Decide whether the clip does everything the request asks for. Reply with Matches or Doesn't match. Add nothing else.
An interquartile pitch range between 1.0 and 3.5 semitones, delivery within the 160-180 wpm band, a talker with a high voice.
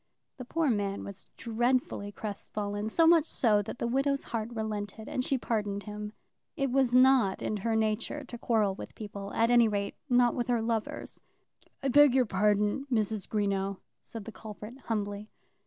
Matches